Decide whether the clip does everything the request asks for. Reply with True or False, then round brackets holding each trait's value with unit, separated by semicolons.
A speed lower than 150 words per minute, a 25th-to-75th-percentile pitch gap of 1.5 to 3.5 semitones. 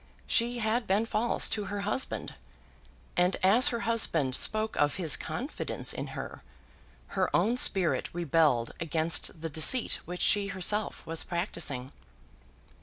False (135 wpm; 5.2 semitones)